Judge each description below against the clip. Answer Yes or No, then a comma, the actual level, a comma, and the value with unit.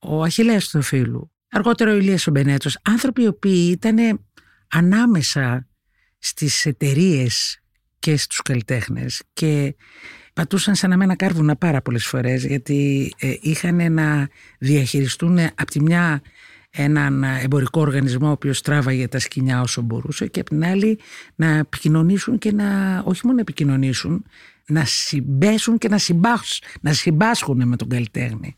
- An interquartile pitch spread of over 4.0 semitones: Yes, average, 5.3 semitones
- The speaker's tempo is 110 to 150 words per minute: Yes, average, 135 wpm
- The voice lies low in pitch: No, medium, 150 Hz